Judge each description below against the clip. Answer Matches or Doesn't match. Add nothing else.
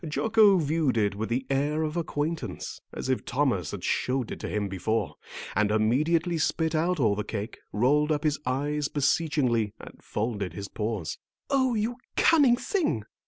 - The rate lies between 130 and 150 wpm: Doesn't match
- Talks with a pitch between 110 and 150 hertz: Matches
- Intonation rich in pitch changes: Matches